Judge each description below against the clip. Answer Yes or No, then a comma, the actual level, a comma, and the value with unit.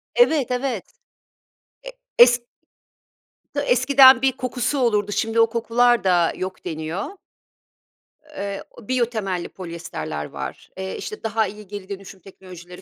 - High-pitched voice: Yes, high, 210 Hz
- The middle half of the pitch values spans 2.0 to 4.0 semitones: No, average, 4.7 semitones